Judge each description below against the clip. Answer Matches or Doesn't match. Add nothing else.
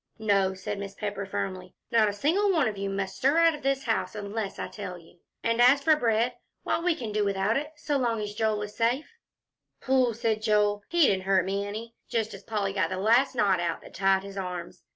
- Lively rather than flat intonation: Doesn't match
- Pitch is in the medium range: Doesn't match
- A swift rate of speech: Matches